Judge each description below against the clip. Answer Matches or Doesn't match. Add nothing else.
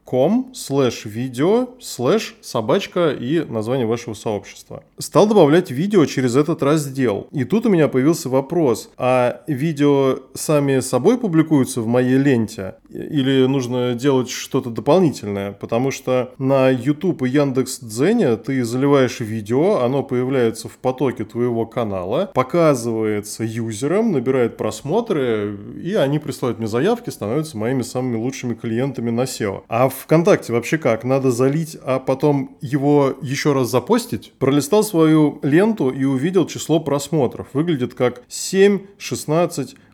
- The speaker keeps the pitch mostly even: Doesn't match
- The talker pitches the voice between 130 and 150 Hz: Matches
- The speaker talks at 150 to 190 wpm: Doesn't match